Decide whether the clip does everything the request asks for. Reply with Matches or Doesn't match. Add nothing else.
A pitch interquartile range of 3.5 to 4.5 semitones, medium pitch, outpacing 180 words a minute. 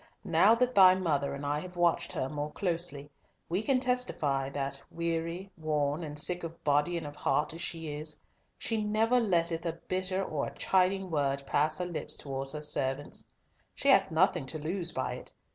Matches